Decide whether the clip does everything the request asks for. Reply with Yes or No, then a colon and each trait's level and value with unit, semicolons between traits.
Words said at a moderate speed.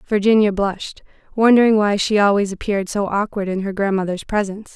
Yes: average, 165 wpm